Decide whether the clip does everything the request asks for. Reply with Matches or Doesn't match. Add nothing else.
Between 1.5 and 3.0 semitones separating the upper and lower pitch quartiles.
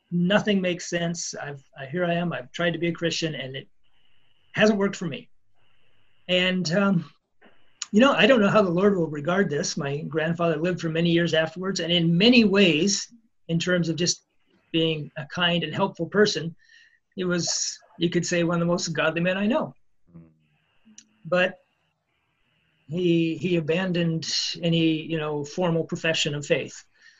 Matches